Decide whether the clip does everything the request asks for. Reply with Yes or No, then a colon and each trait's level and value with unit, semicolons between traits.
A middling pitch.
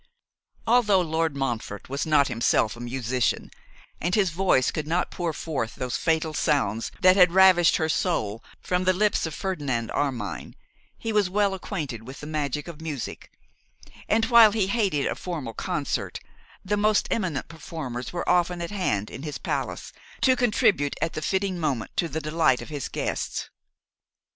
Yes: medium, 160 Hz